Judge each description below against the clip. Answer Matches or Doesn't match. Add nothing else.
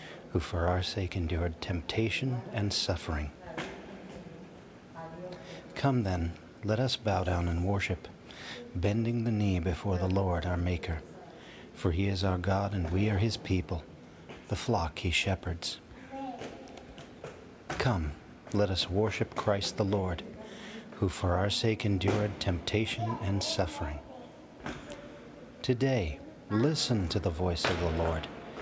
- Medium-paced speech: Doesn't match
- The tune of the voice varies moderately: Matches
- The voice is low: Matches